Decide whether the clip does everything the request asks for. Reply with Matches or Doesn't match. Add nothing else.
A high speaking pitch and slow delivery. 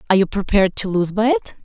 Doesn't match